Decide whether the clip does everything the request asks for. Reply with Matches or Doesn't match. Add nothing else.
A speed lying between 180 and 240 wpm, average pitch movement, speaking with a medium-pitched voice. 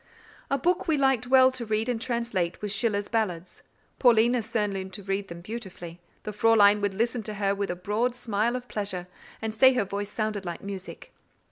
Doesn't match